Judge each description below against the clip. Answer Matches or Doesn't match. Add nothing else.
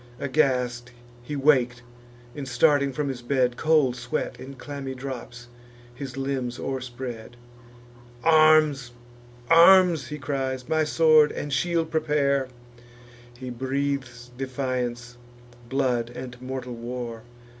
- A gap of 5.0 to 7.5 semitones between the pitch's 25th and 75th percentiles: Doesn't match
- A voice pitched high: Doesn't match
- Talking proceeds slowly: Matches